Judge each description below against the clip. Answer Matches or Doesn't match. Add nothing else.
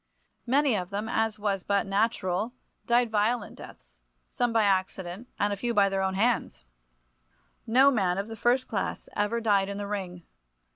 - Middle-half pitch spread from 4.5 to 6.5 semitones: Doesn't match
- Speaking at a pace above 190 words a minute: Doesn't match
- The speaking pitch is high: Matches